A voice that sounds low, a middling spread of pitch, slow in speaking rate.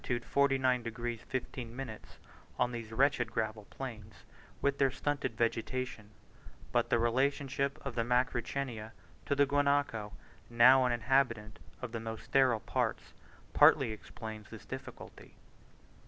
Yes: low, 120 Hz; average, 3.1 semitones; slow, 125 wpm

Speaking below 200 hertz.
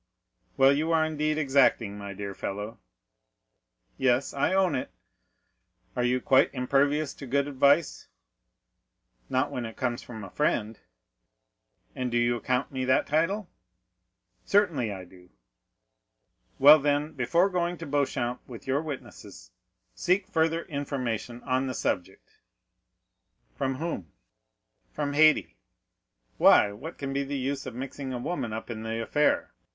Yes: low, 135 Hz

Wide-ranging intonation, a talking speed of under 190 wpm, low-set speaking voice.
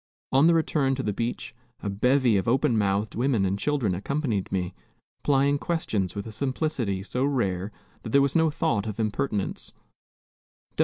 Yes: wide, 5.7 semitones; average, 165 wpm; low, 115 Hz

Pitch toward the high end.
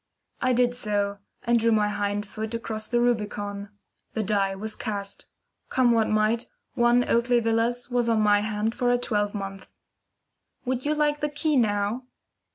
Yes: high, 225 Hz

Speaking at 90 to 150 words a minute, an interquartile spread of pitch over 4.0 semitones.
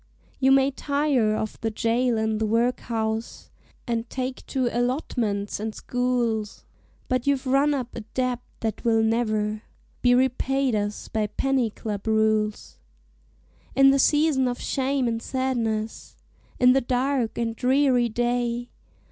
No: average, 140 wpm; average, 3.0 semitones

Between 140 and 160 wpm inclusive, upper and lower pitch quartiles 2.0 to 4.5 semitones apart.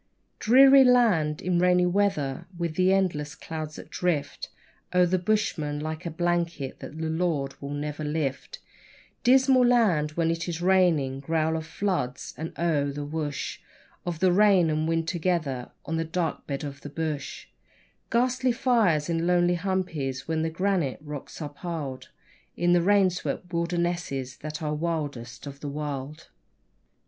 Yes: average, 155 wpm; average, 3.4 semitones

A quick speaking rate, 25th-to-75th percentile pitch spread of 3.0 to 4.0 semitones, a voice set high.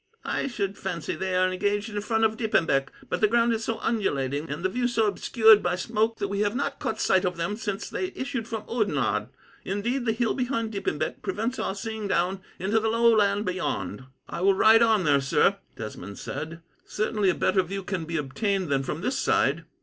Yes: fast, 210 wpm; average, 3.7 semitones; high, 205 Hz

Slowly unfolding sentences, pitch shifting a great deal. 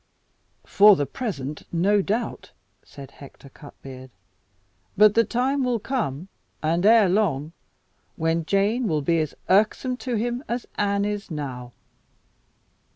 Yes: slow, 130 wpm; wide, 7.1 semitones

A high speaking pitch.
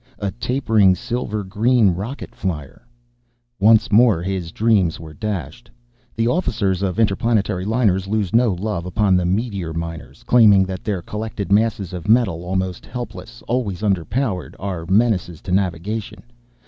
No: low, 100 Hz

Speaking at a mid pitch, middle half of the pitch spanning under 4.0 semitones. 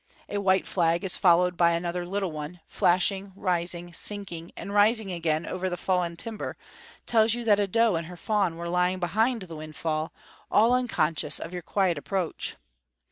Yes: medium, 180 Hz; average, 3.1 semitones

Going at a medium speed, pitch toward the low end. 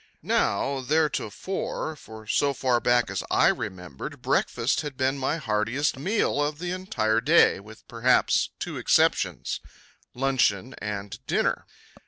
No: slow, 130 wpm; low, 130 Hz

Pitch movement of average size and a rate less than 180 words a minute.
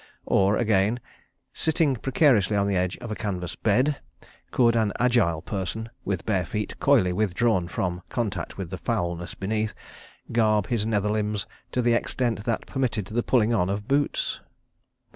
Yes: average, 3.5 semitones; average, 160 wpm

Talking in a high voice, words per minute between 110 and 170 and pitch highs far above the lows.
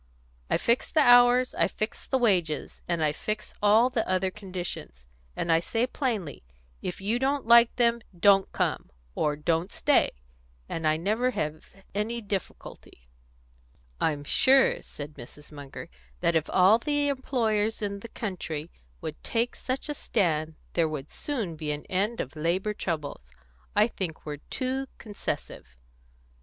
Yes: high, 200 Hz; average, 155 wpm; wide, 7.0 semitones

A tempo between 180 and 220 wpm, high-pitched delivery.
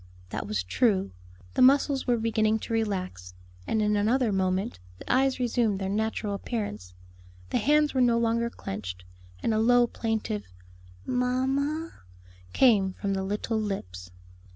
No: average, 145 wpm; high, 220 Hz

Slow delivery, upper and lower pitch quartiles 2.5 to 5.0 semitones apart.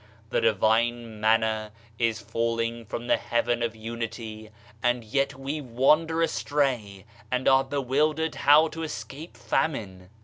Yes: slow, 130 wpm; average, 3.8 semitones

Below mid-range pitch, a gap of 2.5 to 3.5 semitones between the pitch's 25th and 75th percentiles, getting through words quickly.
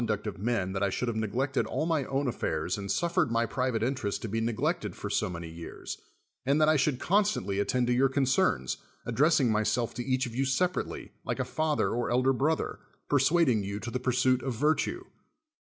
No: low, 125 Hz; average, 4.3 semitones; fast, 210 wpm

